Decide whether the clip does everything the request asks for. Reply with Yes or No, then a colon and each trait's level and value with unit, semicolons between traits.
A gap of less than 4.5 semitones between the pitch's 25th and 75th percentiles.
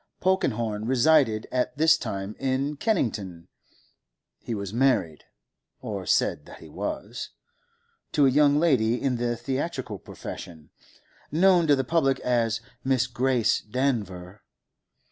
No: average, 5.2 semitones